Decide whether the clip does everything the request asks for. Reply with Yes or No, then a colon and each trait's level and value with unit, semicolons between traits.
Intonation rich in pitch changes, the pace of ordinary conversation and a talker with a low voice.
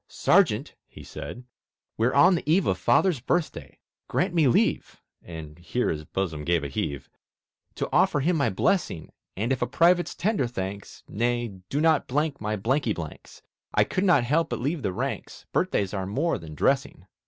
Yes: wide, 9.0 semitones; average, 175 wpm; low, 120 Hz